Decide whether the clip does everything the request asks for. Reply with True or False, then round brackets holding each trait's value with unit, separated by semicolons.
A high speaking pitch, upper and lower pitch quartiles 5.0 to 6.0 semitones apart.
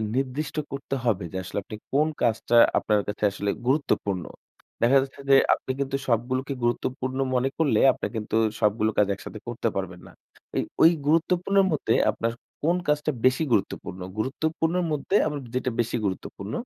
False (130 Hz; 5.4 semitones)